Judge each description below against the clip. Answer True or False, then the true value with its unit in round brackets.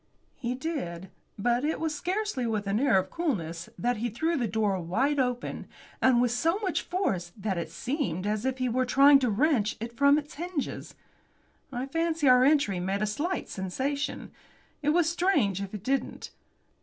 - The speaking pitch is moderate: False (255 Hz)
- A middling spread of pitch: False (6.2 semitones)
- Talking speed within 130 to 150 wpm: False (180 wpm)